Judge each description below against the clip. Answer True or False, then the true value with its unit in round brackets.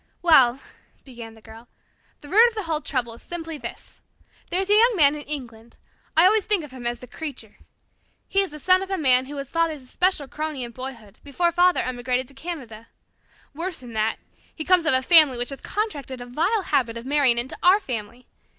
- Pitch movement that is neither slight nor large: False (6.0 semitones)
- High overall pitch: True (280 Hz)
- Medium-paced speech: False (215 wpm)